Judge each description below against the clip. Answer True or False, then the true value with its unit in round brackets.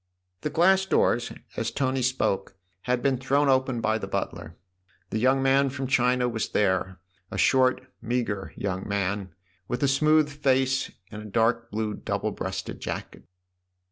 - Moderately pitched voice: False (125 Hz)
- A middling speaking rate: True (155 wpm)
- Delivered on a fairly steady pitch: False (3.8 semitones)